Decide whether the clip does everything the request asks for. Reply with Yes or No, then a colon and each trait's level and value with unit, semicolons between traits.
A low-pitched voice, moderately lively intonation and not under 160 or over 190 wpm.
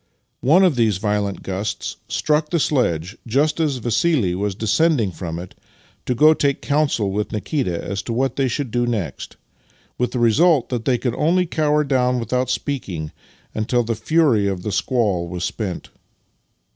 No: low, 120 Hz; wide, 5.9 semitones; average, 170 wpm